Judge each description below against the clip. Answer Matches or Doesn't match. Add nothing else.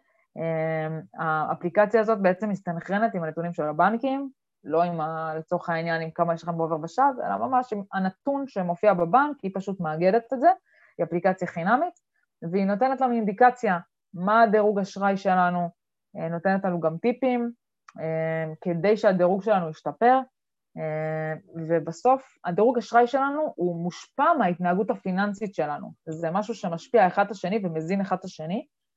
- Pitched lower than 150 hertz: Doesn't match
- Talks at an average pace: Matches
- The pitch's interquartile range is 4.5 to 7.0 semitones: Matches